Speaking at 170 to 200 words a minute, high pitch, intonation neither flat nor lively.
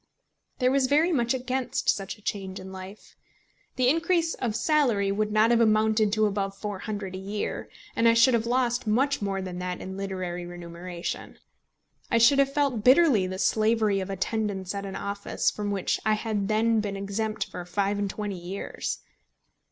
Yes: average, 180 wpm; high, 210 Hz; average, 3.2 semitones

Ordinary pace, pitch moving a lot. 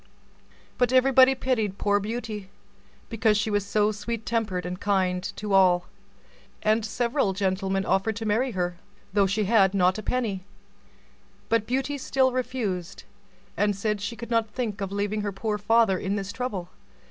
No: average, 160 wpm; average, 3.1 semitones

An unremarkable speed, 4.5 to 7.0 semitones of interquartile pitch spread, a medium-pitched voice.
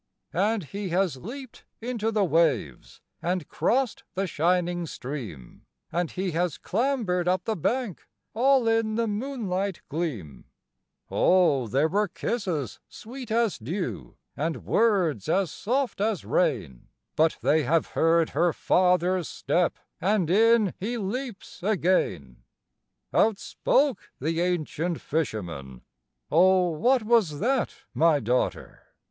No: slow, 125 wpm; wide, 5.6 semitones; medium, 180 Hz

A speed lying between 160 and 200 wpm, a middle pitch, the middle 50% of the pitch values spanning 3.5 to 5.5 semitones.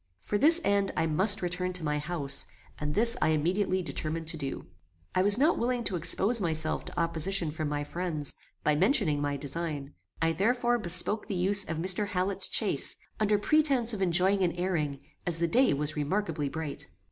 Yes: average, 185 wpm; medium, 175 Hz; average, 4.7 semitones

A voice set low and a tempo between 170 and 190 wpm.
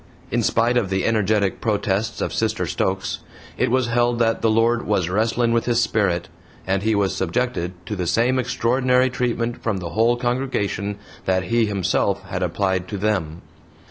Yes: low, 110 Hz; average, 175 wpm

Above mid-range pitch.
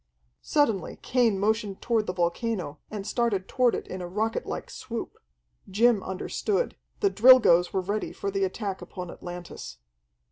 Yes: high, 205 Hz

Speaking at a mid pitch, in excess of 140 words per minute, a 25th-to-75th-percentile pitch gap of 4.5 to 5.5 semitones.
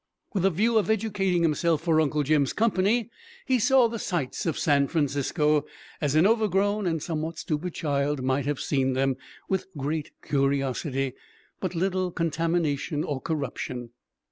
Yes: medium, 160 Hz; average, 155 wpm; average, 5.0 semitones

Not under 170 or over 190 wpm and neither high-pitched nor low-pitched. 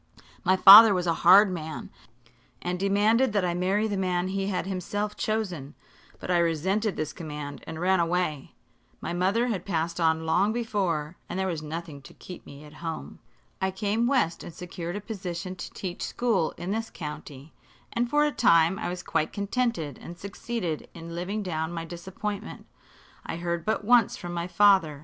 Yes: average, 180 wpm; medium, 180 Hz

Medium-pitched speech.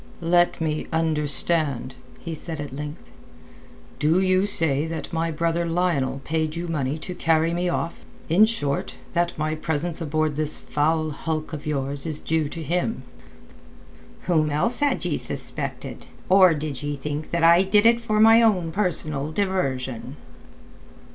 Yes: medium, 160 Hz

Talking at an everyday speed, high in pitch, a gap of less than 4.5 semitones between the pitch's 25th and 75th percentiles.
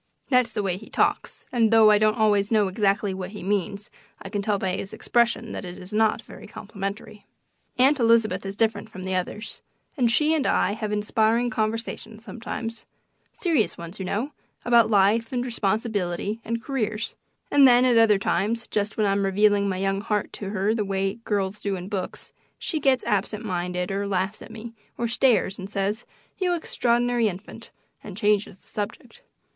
Yes: average, 185 wpm; high, 210 Hz; average, 2.8 semitones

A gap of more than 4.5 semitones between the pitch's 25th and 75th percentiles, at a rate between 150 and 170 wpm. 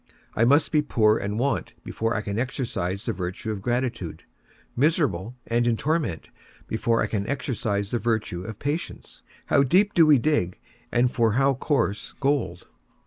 Yes: average, 5.0 semitones; average, 165 wpm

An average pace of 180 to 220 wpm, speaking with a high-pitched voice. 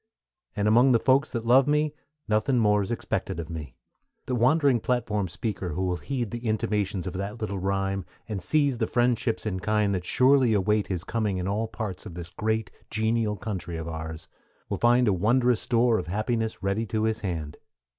No: average, 190 wpm; low, 110 Hz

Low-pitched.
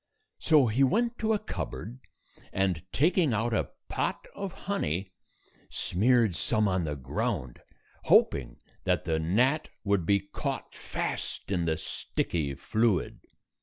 Yes: low, 105 Hz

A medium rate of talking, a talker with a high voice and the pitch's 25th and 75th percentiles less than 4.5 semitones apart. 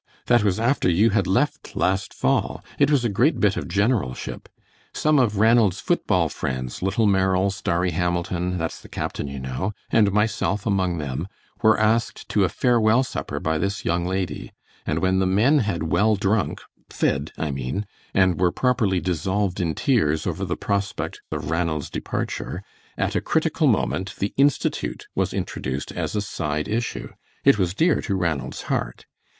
No: average, 170 wpm; very low, 95 Hz; average, 4.1 semitones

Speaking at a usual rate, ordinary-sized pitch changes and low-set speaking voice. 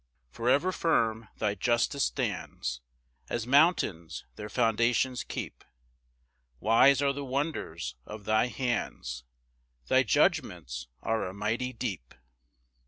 No: slow, 115 wpm; average, 4.2 semitones; low, 115 Hz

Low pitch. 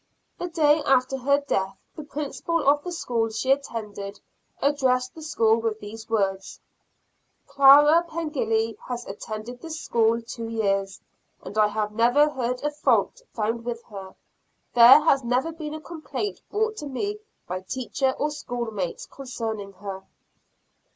No: high, 245 Hz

